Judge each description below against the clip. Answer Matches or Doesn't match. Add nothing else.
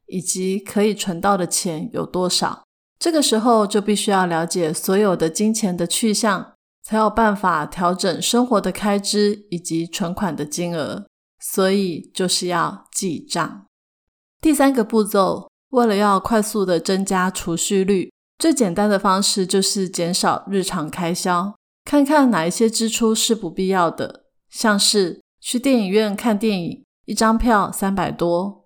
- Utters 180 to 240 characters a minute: Matches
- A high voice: Matches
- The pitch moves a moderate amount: Matches